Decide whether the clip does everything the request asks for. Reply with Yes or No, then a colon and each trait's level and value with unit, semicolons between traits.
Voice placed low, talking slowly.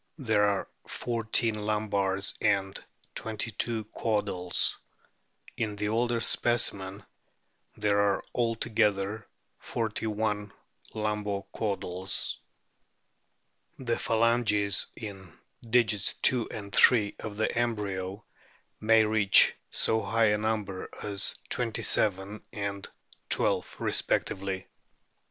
Yes: low, 105 Hz; slow, 95 wpm